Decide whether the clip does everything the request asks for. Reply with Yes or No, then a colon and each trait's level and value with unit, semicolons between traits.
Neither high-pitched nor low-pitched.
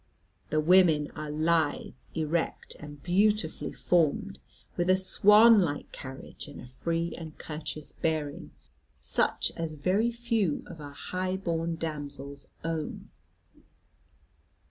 Yes: medium, 165 Hz